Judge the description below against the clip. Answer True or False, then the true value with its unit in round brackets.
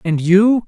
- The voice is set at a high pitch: True (195 Hz)